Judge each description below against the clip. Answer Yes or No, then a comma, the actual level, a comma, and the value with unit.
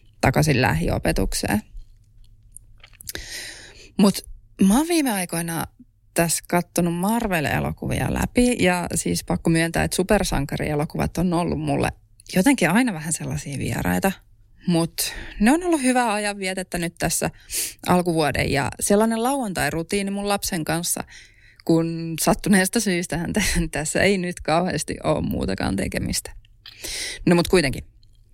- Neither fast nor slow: Yes, average, 115 wpm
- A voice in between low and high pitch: Yes, medium, 170 Hz